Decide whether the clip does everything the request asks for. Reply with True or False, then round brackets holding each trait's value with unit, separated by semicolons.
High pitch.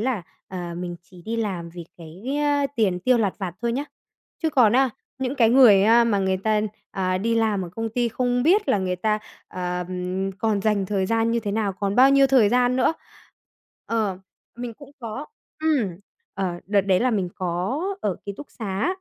True (215 Hz)